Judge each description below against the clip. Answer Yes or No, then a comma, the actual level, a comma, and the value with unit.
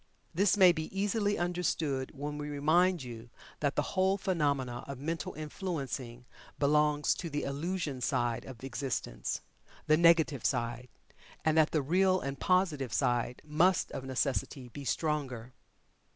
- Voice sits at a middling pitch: Yes, medium, 150 Hz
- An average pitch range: Yes, average, 4.6 semitones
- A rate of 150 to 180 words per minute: No, average, 140 wpm